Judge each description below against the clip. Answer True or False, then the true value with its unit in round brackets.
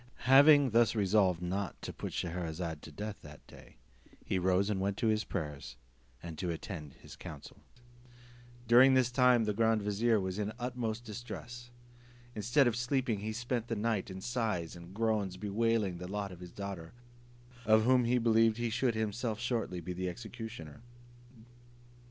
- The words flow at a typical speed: True (170 wpm)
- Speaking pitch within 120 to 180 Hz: False (110 Hz)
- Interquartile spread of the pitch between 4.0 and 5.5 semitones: True (4.3 semitones)